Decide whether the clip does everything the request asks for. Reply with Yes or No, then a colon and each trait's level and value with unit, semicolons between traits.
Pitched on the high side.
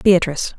No: medium, 175 Hz